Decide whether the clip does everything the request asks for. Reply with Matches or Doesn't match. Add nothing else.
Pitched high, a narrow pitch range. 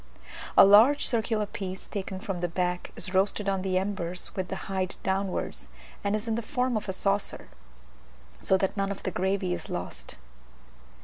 Matches